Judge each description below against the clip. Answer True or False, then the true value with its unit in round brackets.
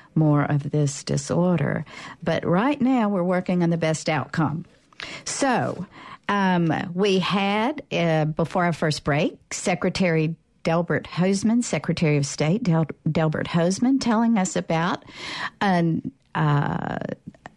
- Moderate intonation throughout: True (3.4 semitones)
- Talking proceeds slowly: True (125 wpm)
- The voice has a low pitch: False (170 Hz)